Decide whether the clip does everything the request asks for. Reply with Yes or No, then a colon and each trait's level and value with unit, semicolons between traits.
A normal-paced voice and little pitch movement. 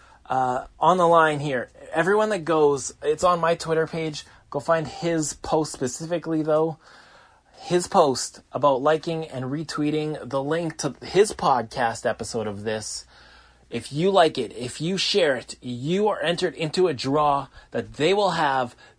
No: average, 160 wpm; average, 3.1 semitones